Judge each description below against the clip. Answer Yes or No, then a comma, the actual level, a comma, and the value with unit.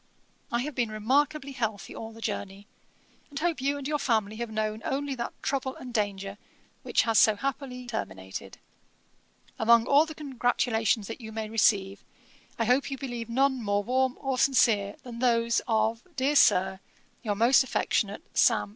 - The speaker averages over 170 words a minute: No, average, 165 wpm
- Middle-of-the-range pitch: No, high, 235 Hz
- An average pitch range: Yes, average, 3.6 semitones